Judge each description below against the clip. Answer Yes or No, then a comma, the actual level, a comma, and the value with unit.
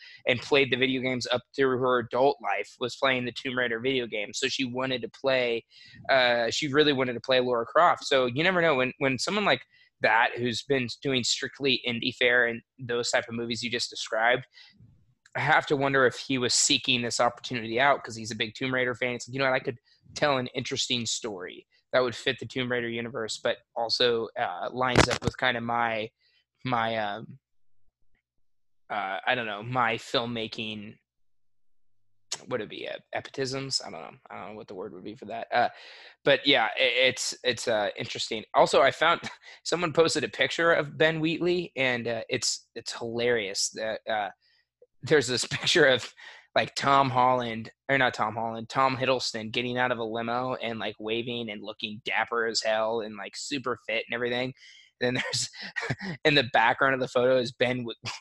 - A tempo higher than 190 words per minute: Yes, average, 200 wpm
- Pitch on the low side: Yes, low, 125 Hz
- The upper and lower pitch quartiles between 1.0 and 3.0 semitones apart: Yes, narrow, 2.6 semitones